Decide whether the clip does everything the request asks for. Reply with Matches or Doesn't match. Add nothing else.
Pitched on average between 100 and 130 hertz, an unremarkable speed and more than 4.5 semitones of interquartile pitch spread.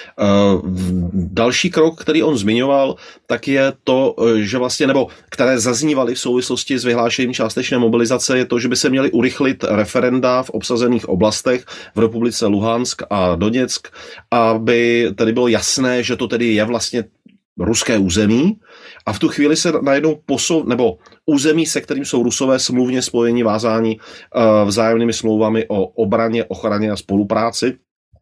Doesn't match